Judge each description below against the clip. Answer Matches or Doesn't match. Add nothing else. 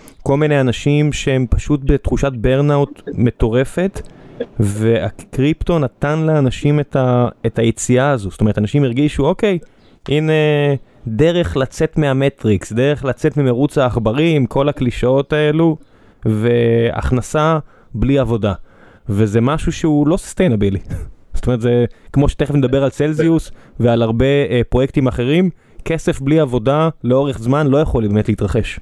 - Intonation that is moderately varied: Matches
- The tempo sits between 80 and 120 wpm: Doesn't match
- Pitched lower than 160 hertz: Matches